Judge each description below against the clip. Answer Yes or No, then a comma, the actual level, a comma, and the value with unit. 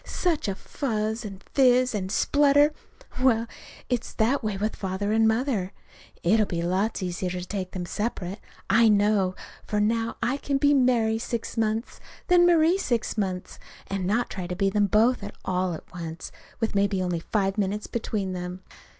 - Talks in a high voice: Yes, high, 215 Hz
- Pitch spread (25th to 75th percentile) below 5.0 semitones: Yes, average, 4.0 semitones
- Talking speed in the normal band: Yes, average, 170 wpm